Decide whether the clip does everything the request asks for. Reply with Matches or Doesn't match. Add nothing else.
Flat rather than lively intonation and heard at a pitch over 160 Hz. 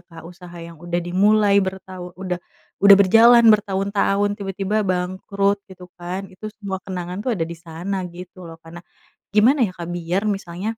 Matches